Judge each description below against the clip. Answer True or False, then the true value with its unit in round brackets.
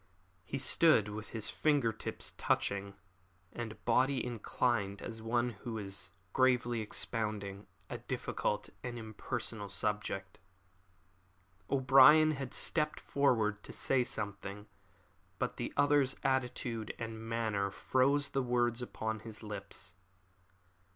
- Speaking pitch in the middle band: False (115 Hz)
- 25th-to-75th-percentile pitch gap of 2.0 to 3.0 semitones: False (3.6 semitones)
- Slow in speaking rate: True (115 wpm)